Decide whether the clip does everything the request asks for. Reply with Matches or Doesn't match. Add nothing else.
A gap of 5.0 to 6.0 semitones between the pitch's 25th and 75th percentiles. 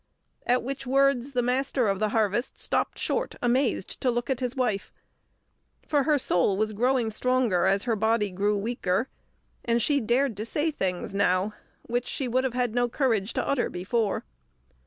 Doesn't match